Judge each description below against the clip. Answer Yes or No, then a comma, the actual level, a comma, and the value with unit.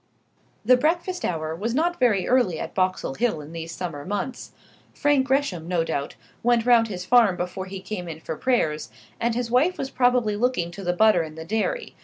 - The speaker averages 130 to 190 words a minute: No, average, 200 wpm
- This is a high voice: Yes, high, 210 Hz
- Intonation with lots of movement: Yes, wide, 6.3 semitones